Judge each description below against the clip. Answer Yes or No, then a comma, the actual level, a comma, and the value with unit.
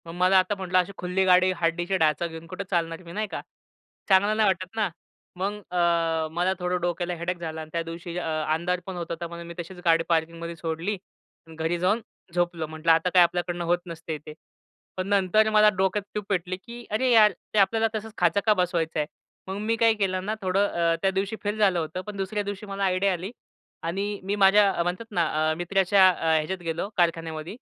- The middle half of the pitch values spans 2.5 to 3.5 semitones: Yes, average, 2.8 semitones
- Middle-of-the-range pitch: Yes, medium, 180 Hz